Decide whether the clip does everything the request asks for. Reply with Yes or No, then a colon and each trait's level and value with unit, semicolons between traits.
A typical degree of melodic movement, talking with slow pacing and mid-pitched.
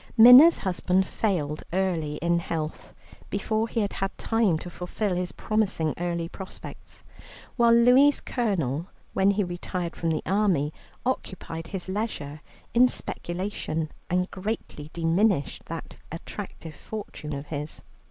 Yes: average, 4.6 semitones; slow, 130 wpm; medium, 180 Hz